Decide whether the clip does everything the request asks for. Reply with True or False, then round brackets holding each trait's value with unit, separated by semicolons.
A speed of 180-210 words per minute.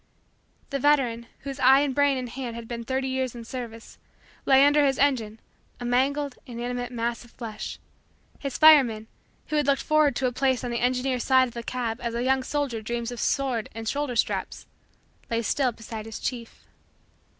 True (190 wpm)